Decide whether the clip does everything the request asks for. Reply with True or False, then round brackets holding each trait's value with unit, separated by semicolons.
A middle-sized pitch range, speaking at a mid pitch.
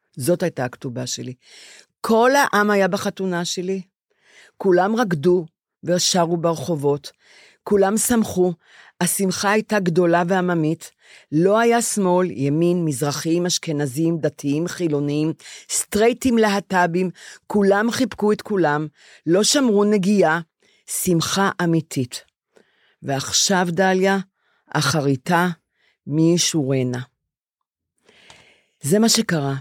True (4.0 semitones; 175 Hz)